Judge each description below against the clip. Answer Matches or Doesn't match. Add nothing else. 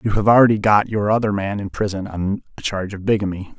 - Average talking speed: Doesn't match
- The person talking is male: Matches